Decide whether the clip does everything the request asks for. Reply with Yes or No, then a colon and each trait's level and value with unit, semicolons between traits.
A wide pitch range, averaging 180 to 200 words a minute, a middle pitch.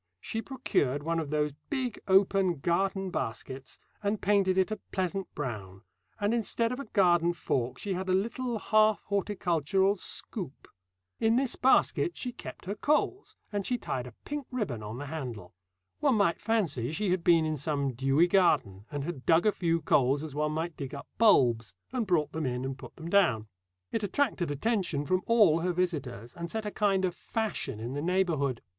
Yes: wide, 6.5 semitones; average, 190 wpm; medium, 175 Hz